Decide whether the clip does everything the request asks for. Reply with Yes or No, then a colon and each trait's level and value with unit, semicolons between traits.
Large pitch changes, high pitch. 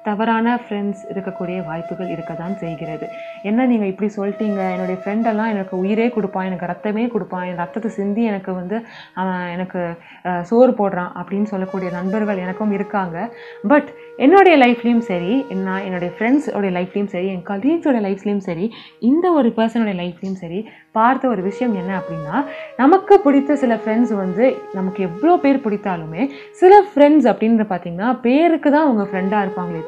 No: average, 4.5 semitones; high, 210 Hz